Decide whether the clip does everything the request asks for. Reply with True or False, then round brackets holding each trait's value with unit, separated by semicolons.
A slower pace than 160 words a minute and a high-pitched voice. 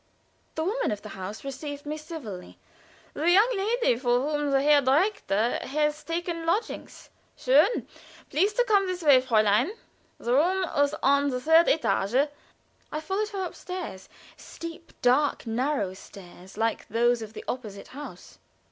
True (150 wpm; 290 Hz)